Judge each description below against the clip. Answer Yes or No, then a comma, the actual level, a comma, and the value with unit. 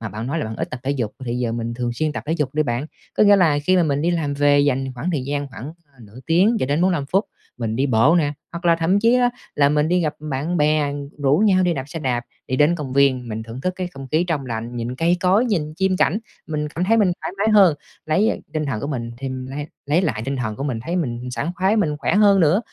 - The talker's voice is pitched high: No, medium, 150 Hz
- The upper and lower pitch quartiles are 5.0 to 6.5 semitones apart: Yes, average, 5.3 semitones